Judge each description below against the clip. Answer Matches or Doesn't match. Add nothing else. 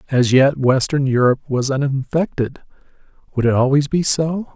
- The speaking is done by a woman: Doesn't match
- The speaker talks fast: Doesn't match